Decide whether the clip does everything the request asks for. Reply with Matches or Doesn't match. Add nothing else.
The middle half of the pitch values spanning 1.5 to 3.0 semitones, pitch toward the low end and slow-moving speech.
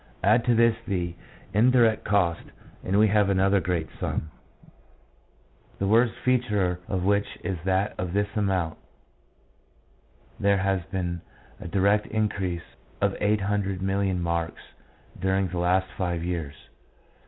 Matches